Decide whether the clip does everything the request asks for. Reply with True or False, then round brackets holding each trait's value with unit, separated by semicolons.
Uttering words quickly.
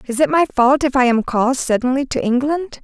True (235 wpm)